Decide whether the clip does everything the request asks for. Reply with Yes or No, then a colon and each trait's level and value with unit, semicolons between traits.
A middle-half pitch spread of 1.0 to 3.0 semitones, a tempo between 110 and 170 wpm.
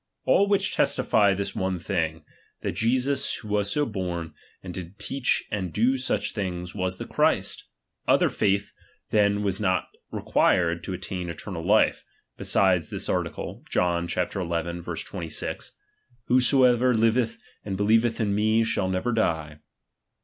No: average, 4.0 semitones; average, 140 wpm